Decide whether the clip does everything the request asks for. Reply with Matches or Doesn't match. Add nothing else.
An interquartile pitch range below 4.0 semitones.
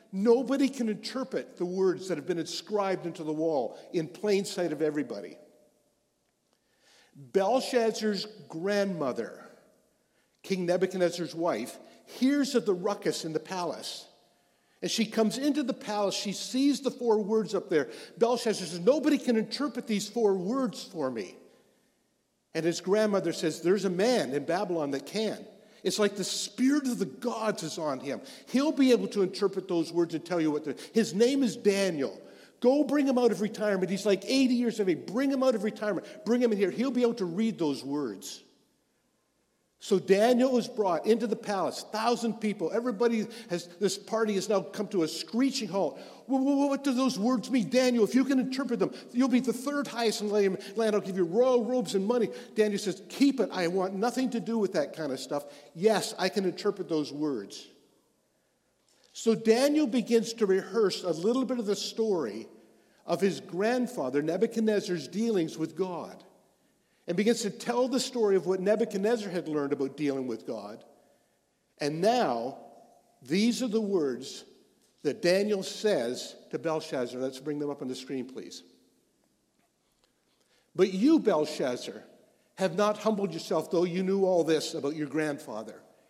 Doesn't match